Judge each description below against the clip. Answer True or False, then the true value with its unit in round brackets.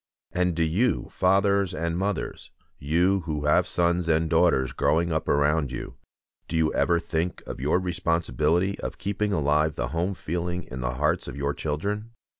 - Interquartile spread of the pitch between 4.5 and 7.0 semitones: False (3.1 semitones)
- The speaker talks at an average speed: True (170 wpm)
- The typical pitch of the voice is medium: False (85 Hz)